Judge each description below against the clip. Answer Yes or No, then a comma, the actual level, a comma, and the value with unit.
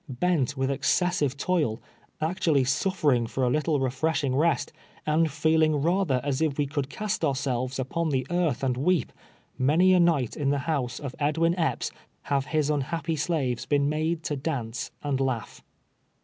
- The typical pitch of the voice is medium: Yes, medium, 145 Hz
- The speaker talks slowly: No, average, 165 wpm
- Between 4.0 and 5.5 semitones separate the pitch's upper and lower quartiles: No, average, 3.6 semitones